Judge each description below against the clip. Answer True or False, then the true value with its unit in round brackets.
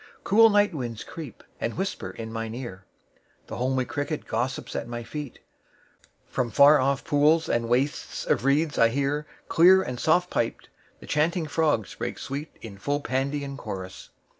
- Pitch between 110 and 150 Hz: True (140 Hz)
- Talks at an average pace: True (145 wpm)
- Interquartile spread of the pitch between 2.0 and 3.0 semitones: False (4.4 semitones)